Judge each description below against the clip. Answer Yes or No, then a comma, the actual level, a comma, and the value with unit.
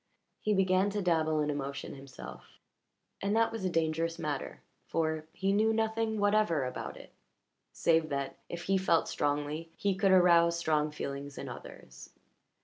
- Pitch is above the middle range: No, medium, 170 Hz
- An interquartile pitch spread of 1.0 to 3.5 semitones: No, average, 4.5 semitones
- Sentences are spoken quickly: No, average, 155 wpm